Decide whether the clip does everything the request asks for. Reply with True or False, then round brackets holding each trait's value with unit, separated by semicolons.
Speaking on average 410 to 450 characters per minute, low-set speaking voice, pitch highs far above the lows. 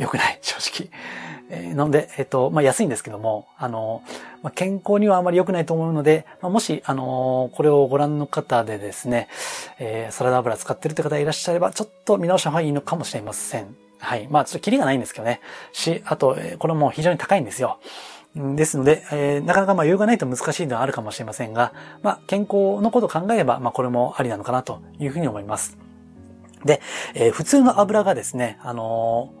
False (445 characters per minute; 145 Hz; 6.2 semitones)